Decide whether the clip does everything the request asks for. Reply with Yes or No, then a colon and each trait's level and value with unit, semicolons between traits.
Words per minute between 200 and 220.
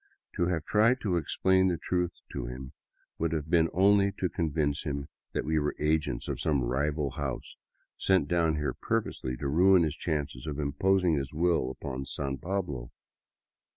No: average, 170 wpm